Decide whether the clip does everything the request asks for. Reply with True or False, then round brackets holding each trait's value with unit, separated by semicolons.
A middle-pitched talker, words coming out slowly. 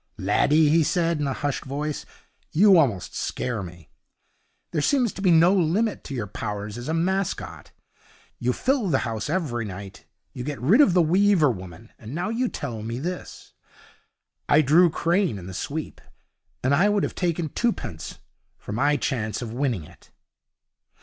False (145 Hz; 170 wpm)